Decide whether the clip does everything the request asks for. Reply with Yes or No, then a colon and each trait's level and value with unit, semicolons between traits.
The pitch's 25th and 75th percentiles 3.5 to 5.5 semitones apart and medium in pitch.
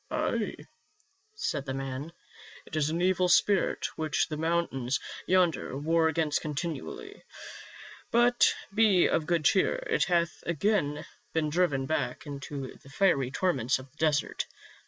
Yes: average, 4.0 semitones; medium, 160 Hz